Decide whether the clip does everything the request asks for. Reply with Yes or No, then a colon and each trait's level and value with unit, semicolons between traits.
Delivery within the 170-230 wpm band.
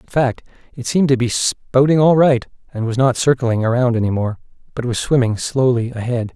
Yes: average, 200 wpm